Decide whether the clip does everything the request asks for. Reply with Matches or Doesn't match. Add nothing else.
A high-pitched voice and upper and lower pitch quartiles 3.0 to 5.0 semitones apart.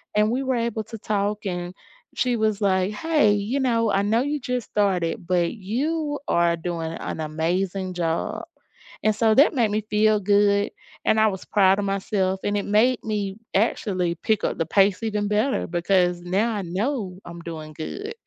Matches